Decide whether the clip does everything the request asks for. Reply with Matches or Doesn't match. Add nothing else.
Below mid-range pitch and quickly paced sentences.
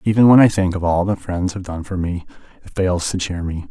Matches